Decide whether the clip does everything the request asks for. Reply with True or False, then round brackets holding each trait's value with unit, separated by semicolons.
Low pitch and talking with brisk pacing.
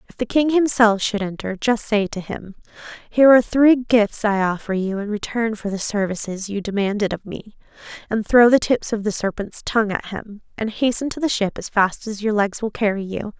False (215 Hz; 220 wpm)